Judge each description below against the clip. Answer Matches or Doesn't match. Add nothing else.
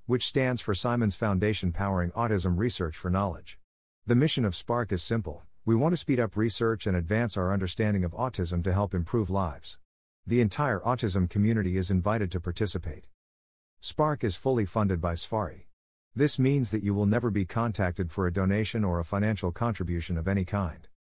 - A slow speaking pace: Doesn't match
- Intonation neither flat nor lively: Matches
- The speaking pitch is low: Matches